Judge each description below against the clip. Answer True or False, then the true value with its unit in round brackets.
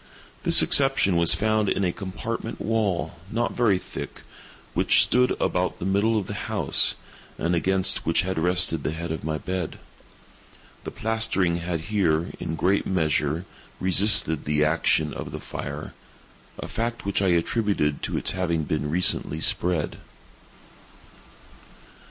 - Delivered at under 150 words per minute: True (140 wpm)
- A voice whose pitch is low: True (90 Hz)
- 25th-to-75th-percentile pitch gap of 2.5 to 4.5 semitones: True (4.2 semitones)